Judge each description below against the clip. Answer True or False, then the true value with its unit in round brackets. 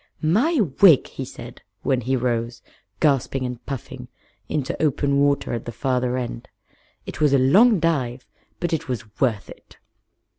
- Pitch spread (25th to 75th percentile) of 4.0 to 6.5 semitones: False (3.4 semitones)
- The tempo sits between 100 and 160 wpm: True (155 wpm)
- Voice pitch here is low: True (130 Hz)